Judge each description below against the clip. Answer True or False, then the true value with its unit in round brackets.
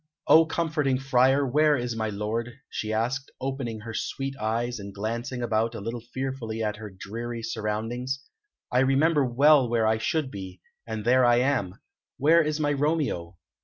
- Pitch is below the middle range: True (120 Hz)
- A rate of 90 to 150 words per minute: False (165 wpm)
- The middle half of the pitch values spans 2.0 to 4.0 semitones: True (3.6 semitones)